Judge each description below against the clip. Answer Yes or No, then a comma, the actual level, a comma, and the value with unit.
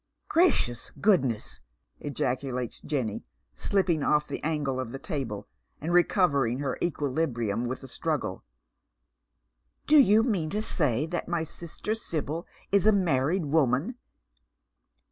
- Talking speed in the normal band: No, slow, 115 wpm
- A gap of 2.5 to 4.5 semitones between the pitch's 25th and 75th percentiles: No, wide, 5.6 semitones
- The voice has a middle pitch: Yes, medium, 150 Hz